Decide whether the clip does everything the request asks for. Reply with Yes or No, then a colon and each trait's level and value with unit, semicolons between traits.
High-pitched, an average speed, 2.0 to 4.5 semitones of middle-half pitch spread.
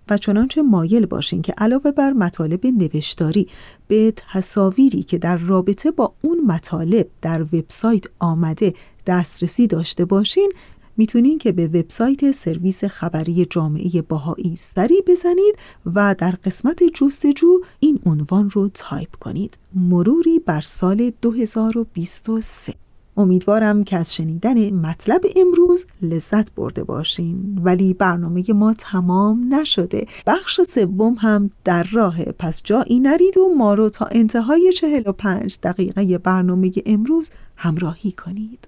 No: high, 200 Hz; average, 125 wpm; wide, 5.4 semitones